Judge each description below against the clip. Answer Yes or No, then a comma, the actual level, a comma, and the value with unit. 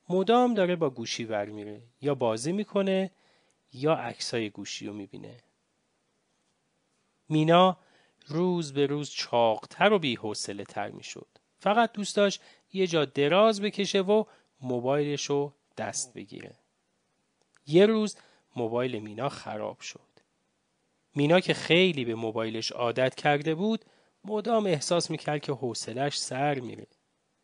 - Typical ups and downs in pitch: No, wide, 7.2 semitones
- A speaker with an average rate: No, slow, 120 wpm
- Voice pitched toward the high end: No, medium, 150 Hz